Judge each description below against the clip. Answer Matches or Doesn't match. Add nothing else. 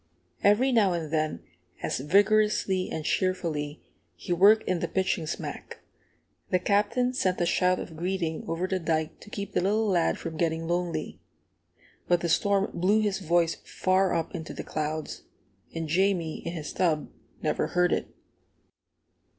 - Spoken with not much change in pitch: Doesn't match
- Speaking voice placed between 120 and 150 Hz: Doesn't match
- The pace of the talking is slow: Doesn't match